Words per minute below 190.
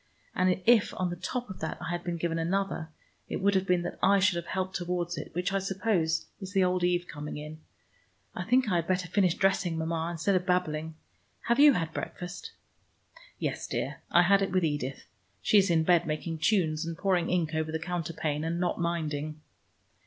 No: fast, 205 wpm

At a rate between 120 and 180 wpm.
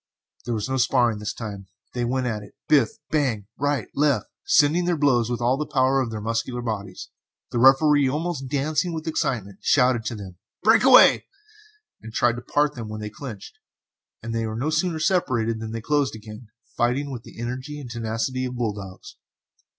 No: average, 200 wpm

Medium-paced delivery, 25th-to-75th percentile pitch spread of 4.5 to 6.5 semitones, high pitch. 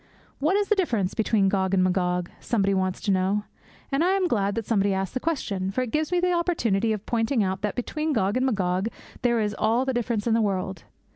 No: fast, 230 wpm; average, 5.2 semitones; high, 215 Hz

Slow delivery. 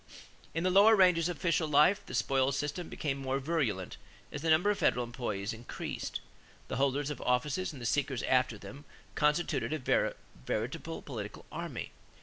No: average, 165 wpm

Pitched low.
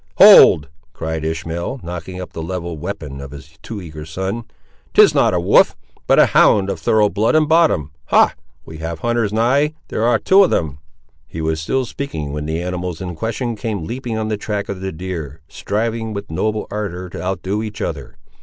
Yes: very low, 95 Hz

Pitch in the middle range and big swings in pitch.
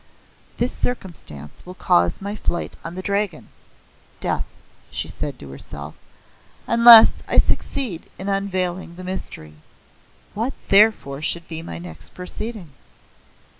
Yes: medium, 180 Hz; wide, 6.1 semitones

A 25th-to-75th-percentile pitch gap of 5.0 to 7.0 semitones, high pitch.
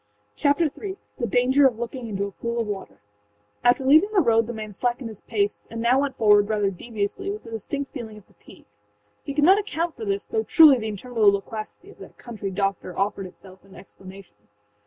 Yes: wide, 5.6 semitones; high, 230 Hz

